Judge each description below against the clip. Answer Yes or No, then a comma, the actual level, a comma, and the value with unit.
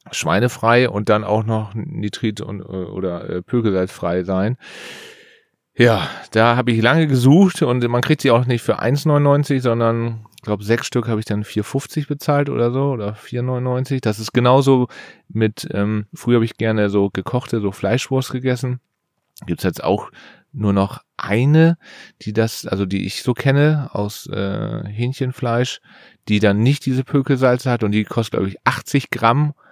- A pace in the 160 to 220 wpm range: Yes, average, 170 wpm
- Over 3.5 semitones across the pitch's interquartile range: Yes, average, 4.1 semitones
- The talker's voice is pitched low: Yes, low, 120 Hz